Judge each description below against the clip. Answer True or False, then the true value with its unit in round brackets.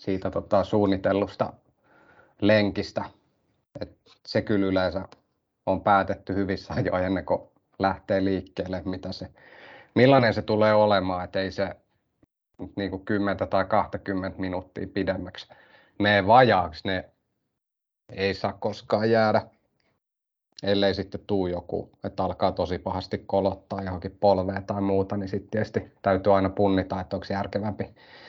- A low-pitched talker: True (100 Hz)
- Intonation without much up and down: True (1.2 semitones)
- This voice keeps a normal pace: True (130 wpm)